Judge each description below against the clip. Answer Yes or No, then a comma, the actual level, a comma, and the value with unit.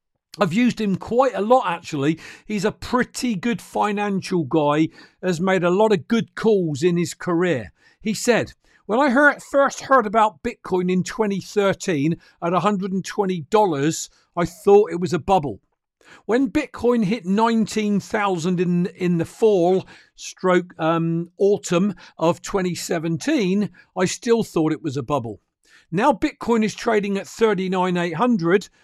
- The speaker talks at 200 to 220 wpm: No, average, 140 wpm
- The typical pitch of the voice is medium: No, high, 195 Hz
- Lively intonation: No, average, 4.0 semitones